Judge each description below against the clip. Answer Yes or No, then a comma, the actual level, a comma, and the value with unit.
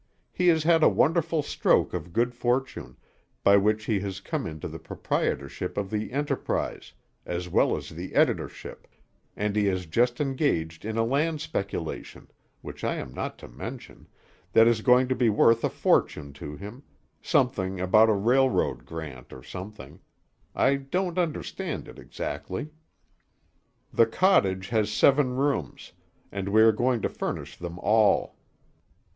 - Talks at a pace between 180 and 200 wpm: No, average, 155 wpm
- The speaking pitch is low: Yes, low, 110 Hz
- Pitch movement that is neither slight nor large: No, wide, 6.1 semitones